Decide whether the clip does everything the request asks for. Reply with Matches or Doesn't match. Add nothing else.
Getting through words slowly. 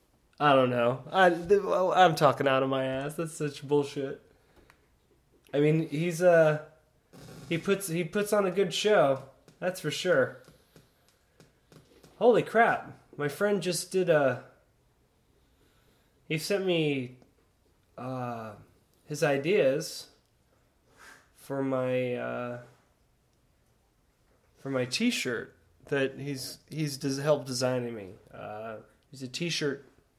Matches